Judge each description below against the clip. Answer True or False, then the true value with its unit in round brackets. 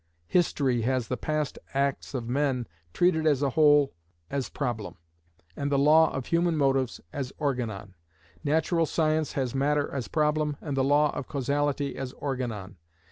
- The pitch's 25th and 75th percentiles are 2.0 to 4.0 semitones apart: True (2.7 semitones)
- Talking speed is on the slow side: False (155 wpm)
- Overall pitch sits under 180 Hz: True (140 Hz)